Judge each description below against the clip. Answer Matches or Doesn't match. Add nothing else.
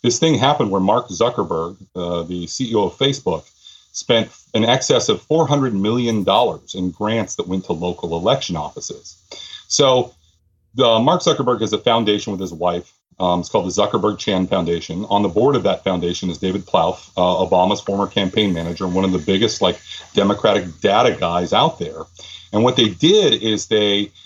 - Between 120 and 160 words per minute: Doesn't match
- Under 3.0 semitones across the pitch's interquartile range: Doesn't match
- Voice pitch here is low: Matches